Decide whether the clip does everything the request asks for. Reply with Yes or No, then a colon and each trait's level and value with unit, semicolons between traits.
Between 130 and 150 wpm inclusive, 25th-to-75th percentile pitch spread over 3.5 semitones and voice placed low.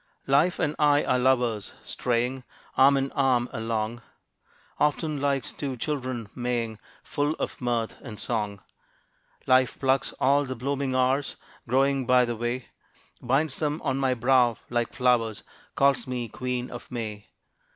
No: average, 140 wpm; narrow, 2.4 semitones; low, 130 Hz